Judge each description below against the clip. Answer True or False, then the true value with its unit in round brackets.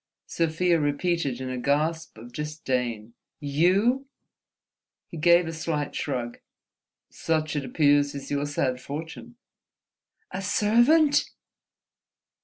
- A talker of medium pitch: True (150 Hz)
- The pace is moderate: False (100 wpm)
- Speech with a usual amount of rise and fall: True (3.7 semitones)